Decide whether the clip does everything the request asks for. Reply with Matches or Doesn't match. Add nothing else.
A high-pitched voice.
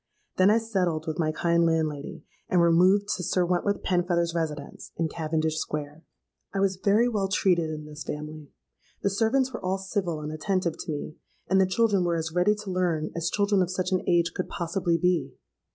Doesn't match